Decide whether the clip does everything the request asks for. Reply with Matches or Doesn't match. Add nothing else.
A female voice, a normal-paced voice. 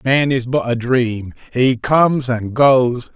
Doesn't match